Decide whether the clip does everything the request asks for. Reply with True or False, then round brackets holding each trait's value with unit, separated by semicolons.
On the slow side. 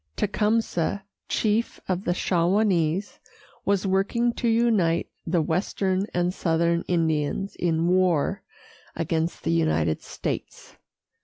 True (105 wpm)